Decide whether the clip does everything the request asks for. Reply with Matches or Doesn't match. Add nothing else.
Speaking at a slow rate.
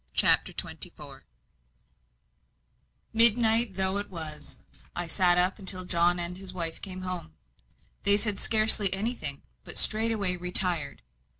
Matches